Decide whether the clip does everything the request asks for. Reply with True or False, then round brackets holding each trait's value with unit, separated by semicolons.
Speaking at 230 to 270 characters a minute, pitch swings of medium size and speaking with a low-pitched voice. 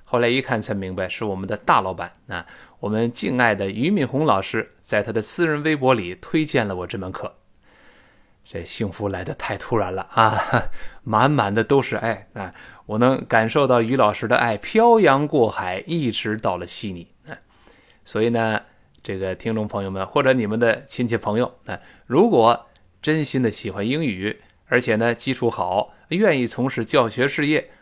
True (260 characters per minute; 4.5 semitones; 115 Hz)